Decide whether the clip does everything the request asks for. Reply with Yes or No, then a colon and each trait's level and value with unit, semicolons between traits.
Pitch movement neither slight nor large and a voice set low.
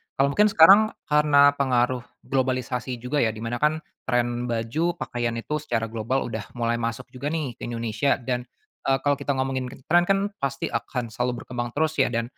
Yes: average, 3.2 semitones; low, 130 Hz